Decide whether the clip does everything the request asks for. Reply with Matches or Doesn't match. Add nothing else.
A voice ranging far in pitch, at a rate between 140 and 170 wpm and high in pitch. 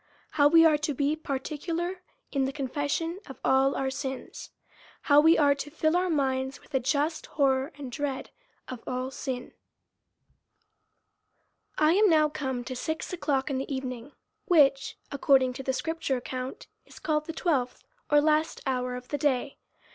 Doesn't match